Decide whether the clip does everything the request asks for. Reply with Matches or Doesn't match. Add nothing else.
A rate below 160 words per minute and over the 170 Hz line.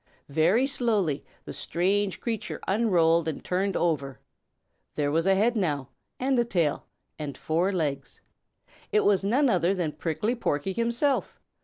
Matches